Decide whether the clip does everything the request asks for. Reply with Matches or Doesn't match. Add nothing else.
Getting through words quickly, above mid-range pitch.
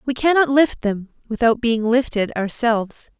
Doesn't match